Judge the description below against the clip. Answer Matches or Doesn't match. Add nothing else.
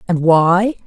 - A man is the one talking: Doesn't match